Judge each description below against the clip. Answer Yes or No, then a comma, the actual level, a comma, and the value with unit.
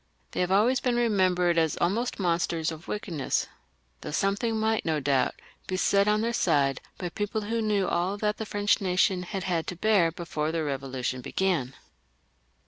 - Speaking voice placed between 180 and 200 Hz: Yes, medium, 185 Hz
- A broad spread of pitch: No, average, 4.3 semitones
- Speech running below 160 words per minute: No, average, 175 wpm